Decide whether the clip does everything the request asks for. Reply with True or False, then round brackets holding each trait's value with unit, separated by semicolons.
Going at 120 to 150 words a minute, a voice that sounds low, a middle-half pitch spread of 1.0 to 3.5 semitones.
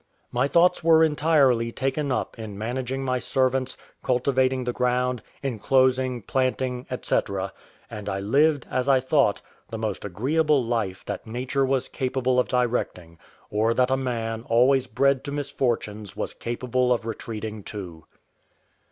True (145 wpm; 125 Hz; 2.8 semitones)